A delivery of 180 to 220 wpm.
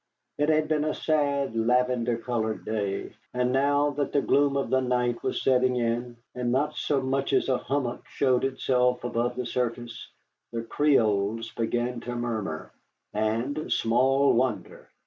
No: average, 155 wpm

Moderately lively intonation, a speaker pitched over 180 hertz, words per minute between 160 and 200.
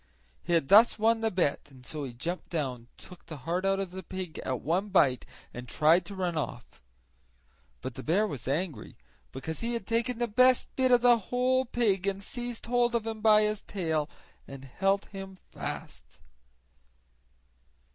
No: wide, 6.6 semitones; high, 190 Hz; average, 180 wpm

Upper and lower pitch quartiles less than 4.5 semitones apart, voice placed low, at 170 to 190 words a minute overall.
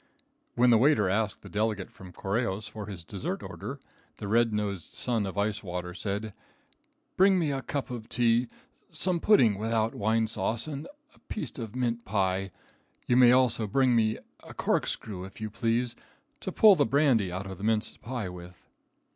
Yes: average, 3.6 semitones; low, 110 Hz; average, 180 wpm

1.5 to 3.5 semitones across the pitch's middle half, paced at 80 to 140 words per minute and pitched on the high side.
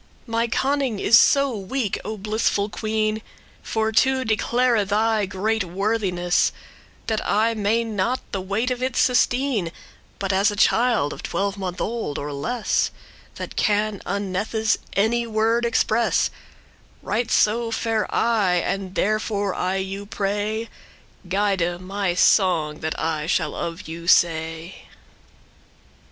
Yes: average, 3.2 semitones; slow, 135 wpm; high, 210 Hz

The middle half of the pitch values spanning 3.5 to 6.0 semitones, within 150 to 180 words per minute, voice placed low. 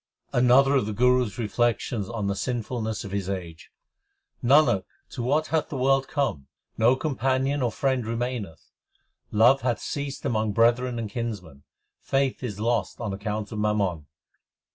Yes: average, 3.8 semitones; average, 160 wpm; low, 120 Hz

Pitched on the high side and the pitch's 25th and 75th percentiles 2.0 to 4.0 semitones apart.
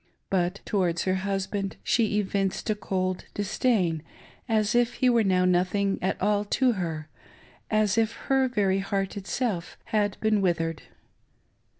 Yes: high, 195 Hz; narrow, 2.5 semitones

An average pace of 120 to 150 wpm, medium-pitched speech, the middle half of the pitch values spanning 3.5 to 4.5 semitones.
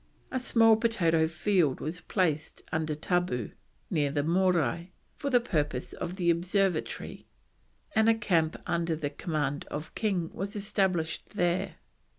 Yes: average, 140 wpm; medium, 175 Hz; average, 3.9 semitones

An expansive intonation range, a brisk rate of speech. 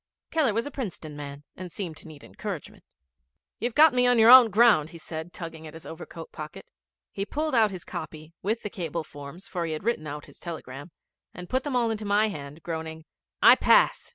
Yes: wide, 6.6 semitones; fast, 215 wpm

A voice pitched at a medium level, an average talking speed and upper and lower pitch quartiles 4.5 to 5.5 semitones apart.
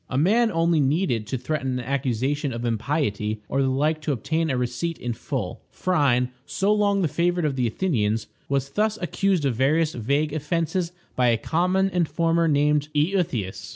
Yes: medium, 145 Hz; average, 175 wpm; average, 5.0 semitones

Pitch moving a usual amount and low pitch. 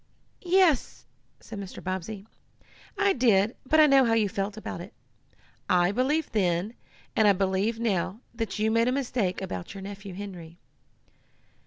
No: average, 3.6 semitones; high, 205 Hz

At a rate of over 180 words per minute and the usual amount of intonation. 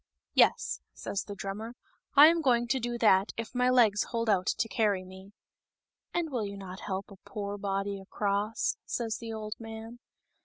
Yes: average, 200 wpm; average, 3.1 semitones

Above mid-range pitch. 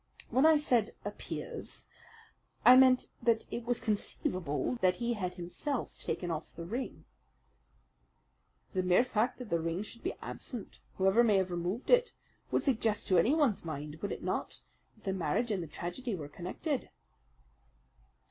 Yes: high, 210 Hz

